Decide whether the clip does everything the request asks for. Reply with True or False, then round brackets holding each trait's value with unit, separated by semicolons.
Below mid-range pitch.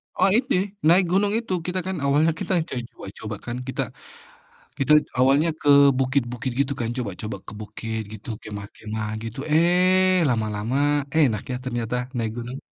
True (130 Hz)